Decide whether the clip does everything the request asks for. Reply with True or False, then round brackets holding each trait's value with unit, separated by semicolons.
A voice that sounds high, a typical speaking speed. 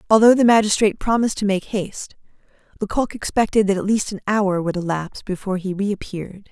True (200 Hz; 175 wpm)